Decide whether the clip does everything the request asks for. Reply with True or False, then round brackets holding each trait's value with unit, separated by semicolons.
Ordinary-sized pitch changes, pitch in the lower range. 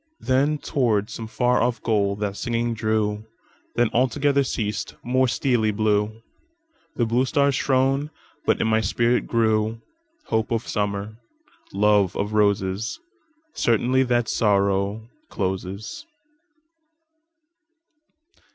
True (3.9 semitones; 115 Hz)